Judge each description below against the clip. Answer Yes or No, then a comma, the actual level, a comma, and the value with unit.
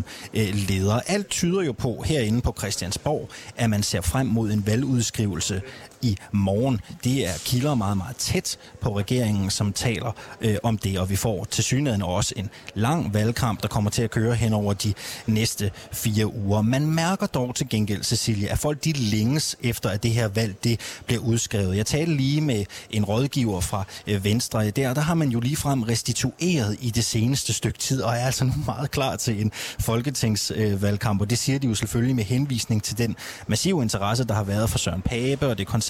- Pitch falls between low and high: No, low, 115 Hz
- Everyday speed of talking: Yes, average, 195 wpm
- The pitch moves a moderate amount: Yes, average, 3.6 semitones